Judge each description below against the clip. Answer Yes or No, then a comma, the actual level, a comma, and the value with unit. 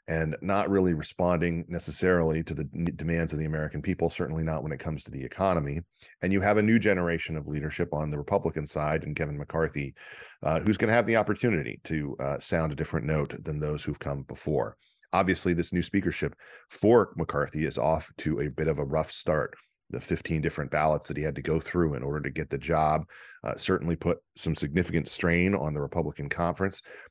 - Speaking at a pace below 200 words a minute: No, fast, 205 wpm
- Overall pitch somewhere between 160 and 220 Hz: No, very low, 80 Hz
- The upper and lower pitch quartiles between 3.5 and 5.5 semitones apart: No, average, 2.7 semitones